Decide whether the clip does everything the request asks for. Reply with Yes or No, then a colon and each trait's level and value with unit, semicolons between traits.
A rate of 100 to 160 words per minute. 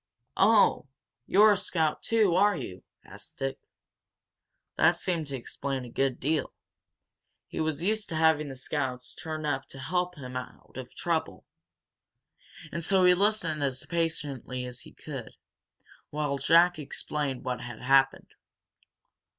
Yes: average, 140 wpm